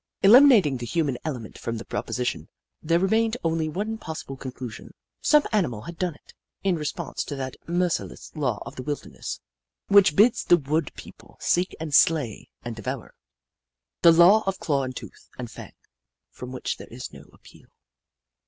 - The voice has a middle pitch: Yes, medium, 160 Hz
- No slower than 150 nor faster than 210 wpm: Yes, average, 170 wpm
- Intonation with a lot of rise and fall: Yes, wide, 6.1 semitones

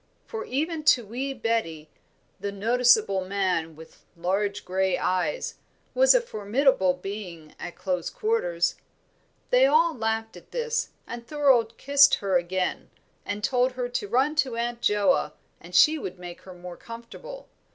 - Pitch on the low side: No, high, 230 Hz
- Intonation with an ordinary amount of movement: No, wide, 6.5 semitones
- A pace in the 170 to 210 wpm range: No, average, 150 wpm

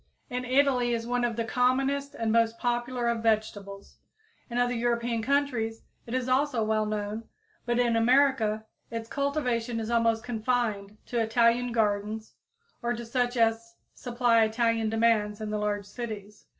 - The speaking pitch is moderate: No, high, 230 Hz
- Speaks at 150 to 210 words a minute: Yes, average, 160 wpm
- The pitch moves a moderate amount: No, narrow, 1.9 semitones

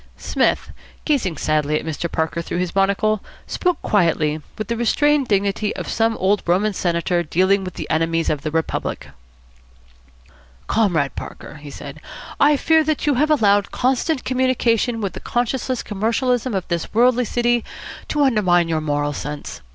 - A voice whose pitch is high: Yes, high, 200 Hz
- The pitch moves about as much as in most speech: No, wide, 6.6 semitones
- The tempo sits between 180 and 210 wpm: No, average, 160 wpm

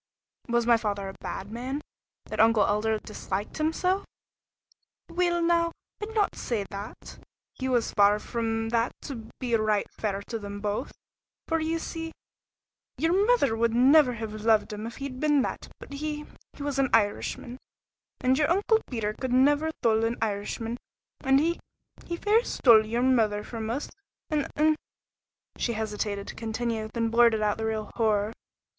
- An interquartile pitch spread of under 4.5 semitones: No, average, 5.1 semitones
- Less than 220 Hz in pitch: No, high, 235 Hz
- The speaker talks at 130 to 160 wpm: No, average, 170 wpm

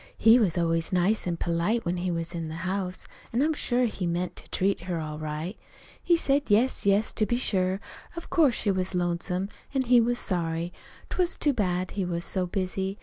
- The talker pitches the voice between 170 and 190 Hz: Yes, medium, 185 Hz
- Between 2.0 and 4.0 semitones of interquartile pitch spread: No, average, 4.6 semitones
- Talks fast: Yes, fast, 210 wpm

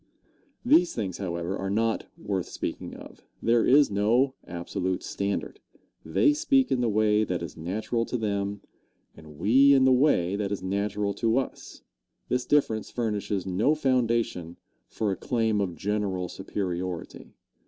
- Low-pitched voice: Yes, low, 105 Hz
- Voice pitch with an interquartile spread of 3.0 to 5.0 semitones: Yes, average, 4.2 semitones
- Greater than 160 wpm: No, average, 150 wpm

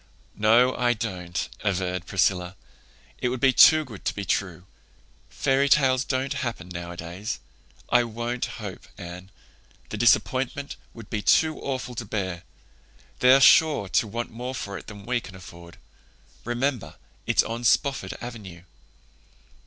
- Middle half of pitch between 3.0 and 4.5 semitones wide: No, wide, 5.5 semitones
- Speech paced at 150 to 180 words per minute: No, average, 140 wpm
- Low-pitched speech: Yes, low, 115 Hz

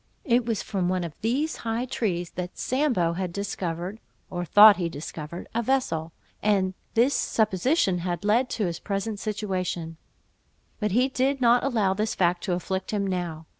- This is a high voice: Yes, high, 195 Hz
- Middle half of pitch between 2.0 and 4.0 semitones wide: No, average, 4.6 semitones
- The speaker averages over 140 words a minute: Yes, average, 170 wpm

